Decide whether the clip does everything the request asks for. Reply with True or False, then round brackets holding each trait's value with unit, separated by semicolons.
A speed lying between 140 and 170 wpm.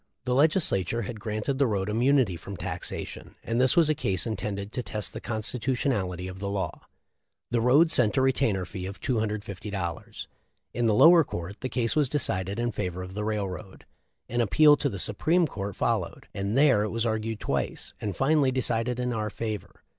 False (185 wpm)